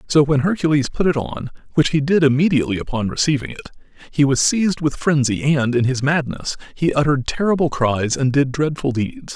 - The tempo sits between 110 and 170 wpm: No, average, 190 wpm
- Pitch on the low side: No, medium, 145 Hz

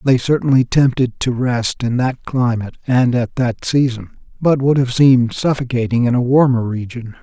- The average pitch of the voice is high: No, low, 125 Hz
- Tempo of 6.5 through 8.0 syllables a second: No, 4.9 syllables/s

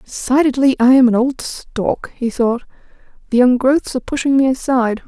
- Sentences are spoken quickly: No, average, 180 wpm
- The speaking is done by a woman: Yes, female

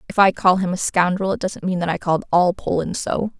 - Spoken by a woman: Yes, female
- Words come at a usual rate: No, fast, 265 wpm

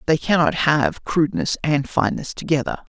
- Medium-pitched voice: Yes, medium, 145 Hz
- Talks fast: No, average, 145 wpm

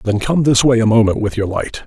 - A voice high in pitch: No, low, 115 Hz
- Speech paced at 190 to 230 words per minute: No, fast, 290 wpm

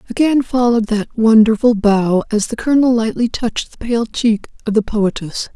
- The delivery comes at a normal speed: Yes, average, 175 wpm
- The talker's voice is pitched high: Yes, high, 225 Hz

